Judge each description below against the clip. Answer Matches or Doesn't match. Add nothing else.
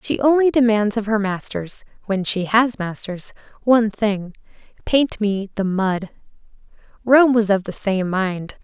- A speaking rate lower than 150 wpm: Matches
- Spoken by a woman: Matches